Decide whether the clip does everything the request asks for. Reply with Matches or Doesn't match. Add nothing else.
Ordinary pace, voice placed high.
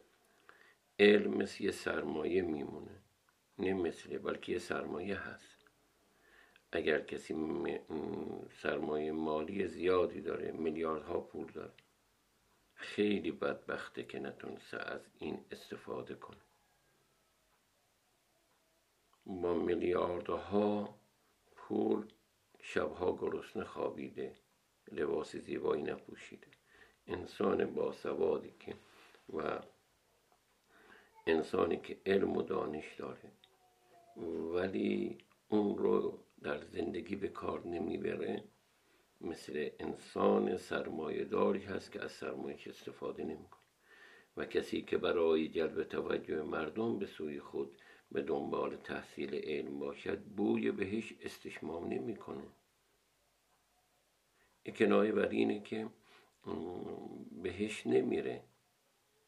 Doesn't match